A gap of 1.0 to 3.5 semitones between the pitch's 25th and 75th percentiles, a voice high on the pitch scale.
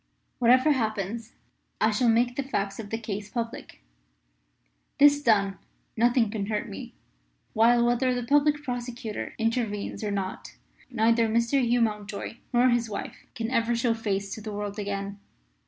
Yes: average, 2.7 semitones; high, 230 Hz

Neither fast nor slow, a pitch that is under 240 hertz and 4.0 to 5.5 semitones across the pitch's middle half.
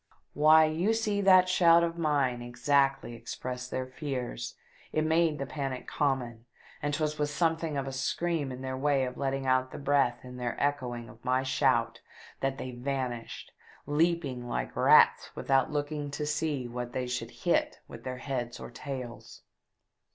No: average, 165 wpm; low, 135 Hz; average, 3.1 semitones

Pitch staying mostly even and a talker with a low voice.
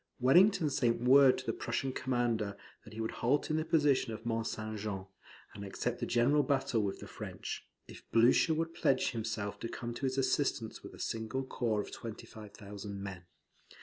No: average, 3.8 semitones; low, 120 Hz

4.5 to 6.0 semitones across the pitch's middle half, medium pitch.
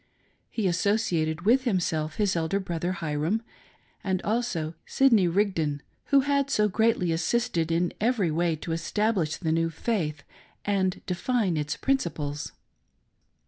Yes: average, 5.1 semitones; medium, 180 Hz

